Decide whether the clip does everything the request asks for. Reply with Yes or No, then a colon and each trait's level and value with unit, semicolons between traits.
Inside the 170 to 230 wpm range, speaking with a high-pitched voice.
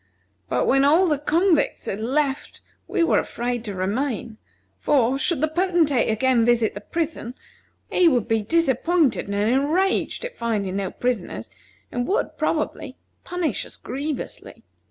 No: average, 145 wpm; very high, 265 Hz